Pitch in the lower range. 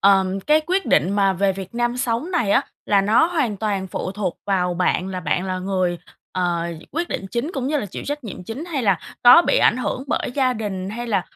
No: high, 205 Hz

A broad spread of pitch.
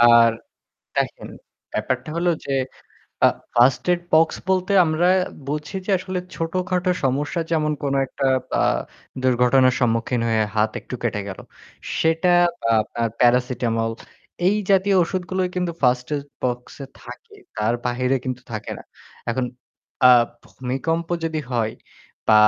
Yes: wide, 5.7 semitones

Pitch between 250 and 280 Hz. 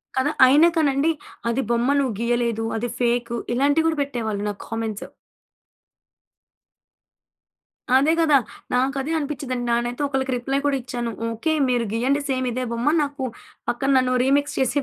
Yes: very high, 255 Hz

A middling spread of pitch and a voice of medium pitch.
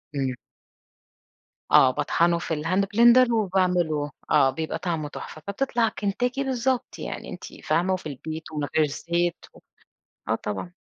No: wide, 5.9 semitones; medium, 170 Hz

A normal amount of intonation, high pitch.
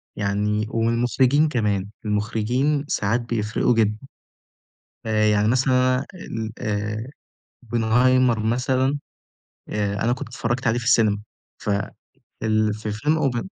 No: average, 3.0 semitones; low, 115 Hz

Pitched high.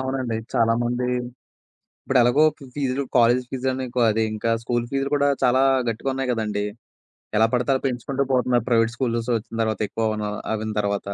No: low, 120 Hz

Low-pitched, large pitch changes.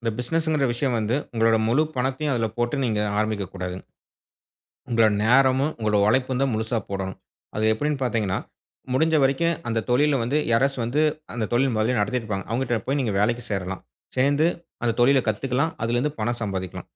No: low, 120 Hz; average, 3.8 semitones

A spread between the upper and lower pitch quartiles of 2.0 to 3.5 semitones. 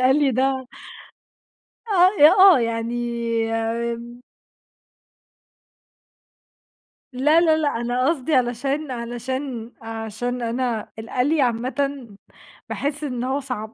Yes: average, 3.1 semitones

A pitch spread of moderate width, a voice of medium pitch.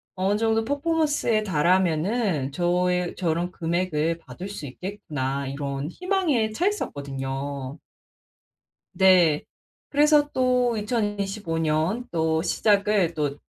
No: wide, 6.2 semitones; medium, 180 Hz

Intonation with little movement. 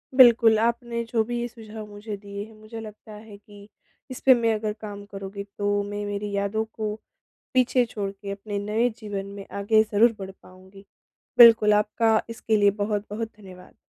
Yes: narrow, 1.9 semitones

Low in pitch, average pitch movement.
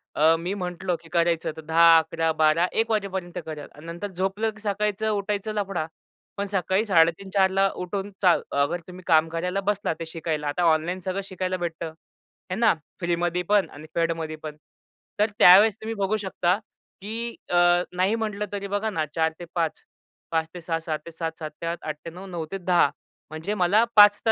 No: medium, 180 Hz; average, 3.3 semitones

